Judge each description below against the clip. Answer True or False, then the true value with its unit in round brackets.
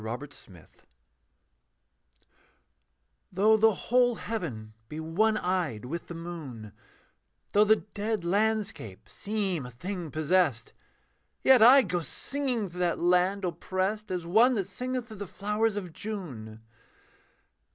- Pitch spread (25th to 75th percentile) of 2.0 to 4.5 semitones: False (5.3 semitones)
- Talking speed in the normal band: False (130 wpm)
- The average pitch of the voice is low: False (185 Hz)